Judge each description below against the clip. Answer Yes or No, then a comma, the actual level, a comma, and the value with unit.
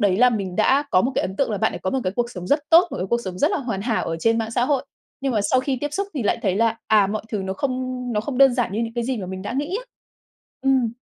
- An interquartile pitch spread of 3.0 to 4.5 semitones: No, average, 4.9 semitones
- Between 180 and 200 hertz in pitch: No, high, 235 Hz